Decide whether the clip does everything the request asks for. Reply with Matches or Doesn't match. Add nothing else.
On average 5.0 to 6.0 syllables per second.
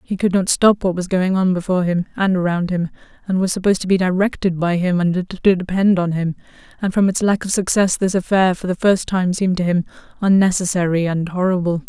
Matches